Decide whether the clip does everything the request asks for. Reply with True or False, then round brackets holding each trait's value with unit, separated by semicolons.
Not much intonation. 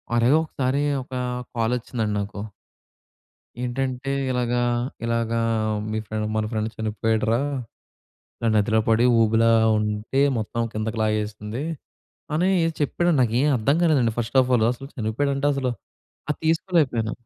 False (3.6 semitones)